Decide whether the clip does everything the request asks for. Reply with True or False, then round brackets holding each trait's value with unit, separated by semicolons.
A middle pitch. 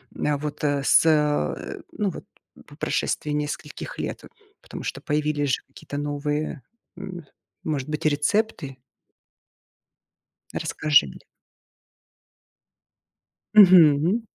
True (150 Hz)